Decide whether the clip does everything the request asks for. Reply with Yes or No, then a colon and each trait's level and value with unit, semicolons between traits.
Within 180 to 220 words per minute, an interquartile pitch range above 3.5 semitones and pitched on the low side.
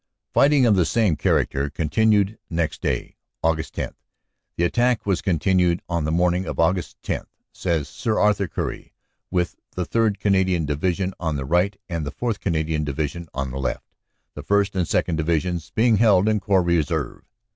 No: average, 170 wpm; average, 4.0 semitones; very low, 90 Hz